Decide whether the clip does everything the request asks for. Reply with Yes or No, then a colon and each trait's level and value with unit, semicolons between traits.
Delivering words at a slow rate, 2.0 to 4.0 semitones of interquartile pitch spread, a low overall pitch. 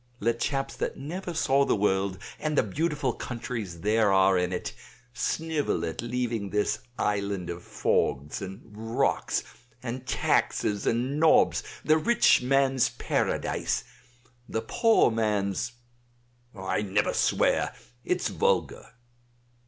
No: slow, 120 wpm; wide, 5.6 semitones; low, 115 Hz